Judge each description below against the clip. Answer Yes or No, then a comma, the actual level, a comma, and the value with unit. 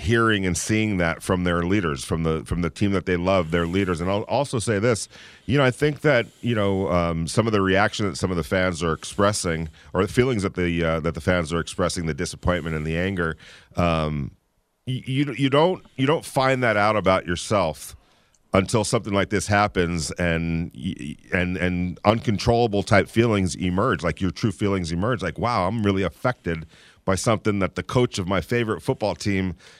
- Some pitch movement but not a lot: Yes, average, 4.1 semitones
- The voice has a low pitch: Yes, very low, 95 Hz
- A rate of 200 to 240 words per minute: Yes, fast, 205 wpm